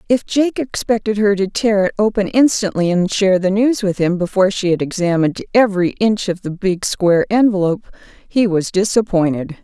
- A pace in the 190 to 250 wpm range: No, average, 180 wpm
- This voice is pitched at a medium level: No, high, 200 Hz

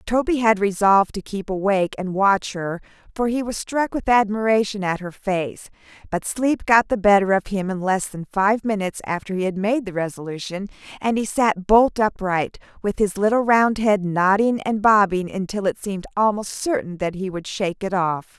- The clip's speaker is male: No, female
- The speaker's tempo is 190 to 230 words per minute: Yes, average, 195 wpm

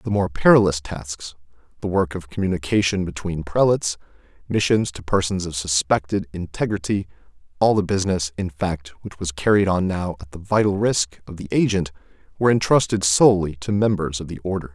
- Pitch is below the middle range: Yes, very low, 90 Hz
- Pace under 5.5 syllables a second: No, 5.6 syllables/s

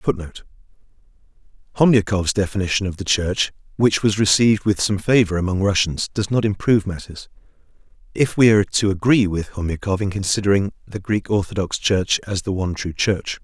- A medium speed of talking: Yes, average, 160 wpm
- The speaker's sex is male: Yes, male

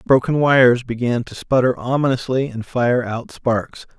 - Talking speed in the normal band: Yes, average, 150 wpm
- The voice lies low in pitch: Yes, low, 125 Hz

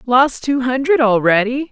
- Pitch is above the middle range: Yes, very high, 255 Hz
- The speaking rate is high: No, average, 140 wpm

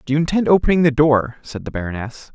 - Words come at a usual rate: No, fast, 230 wpm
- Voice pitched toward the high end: No, medium, 140 Hz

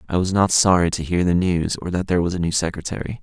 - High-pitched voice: No, very low, 90 Hz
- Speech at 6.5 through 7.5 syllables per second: Yes, 6.6 syllables/s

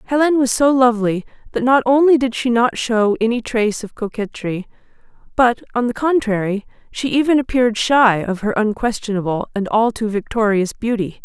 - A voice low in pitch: No, high, 230 Hz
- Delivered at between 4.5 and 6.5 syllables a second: Yes, 5.4 syllables/s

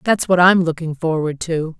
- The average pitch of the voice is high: No, medium, 165 Hz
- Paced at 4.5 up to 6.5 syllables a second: Yes, 4.8 syllables/s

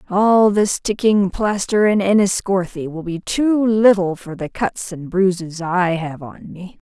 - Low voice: No, high, 190 Hz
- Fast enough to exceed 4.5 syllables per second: No, 4.0 syllables/s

